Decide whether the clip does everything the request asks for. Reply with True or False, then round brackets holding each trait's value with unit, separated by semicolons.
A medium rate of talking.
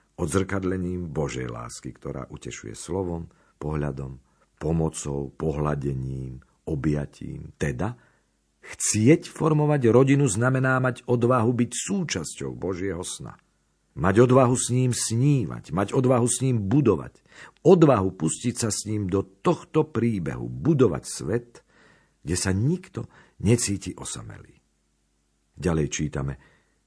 False (105 wpm)